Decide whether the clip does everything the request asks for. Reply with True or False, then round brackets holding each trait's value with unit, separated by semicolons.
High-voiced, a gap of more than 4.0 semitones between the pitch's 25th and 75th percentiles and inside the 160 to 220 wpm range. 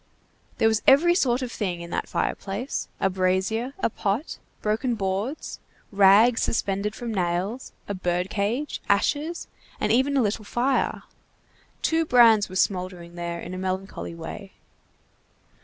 False (205 Hz; 4.7 semitones; 140 wpm)